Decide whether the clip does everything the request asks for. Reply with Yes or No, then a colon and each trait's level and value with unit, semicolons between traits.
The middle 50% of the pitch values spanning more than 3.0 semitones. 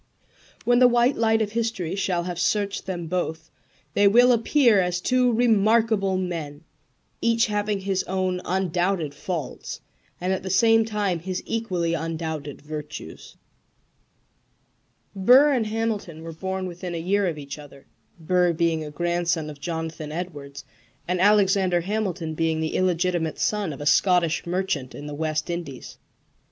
Yes: average, 4.1 semitones